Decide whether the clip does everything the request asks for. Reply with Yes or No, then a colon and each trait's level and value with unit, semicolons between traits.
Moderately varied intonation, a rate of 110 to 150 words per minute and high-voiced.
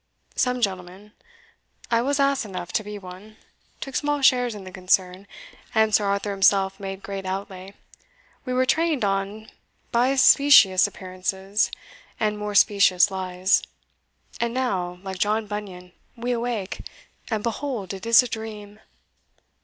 Yes: average, 3.6 semitones; average, 140 wpm; high, 205 Hz